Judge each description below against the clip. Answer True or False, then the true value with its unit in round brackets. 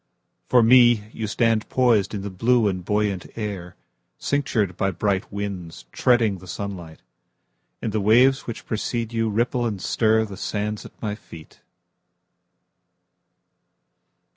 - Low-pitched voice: True (105 Hz)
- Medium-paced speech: False (105 wpm)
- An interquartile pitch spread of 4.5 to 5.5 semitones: False (3.1 semitones)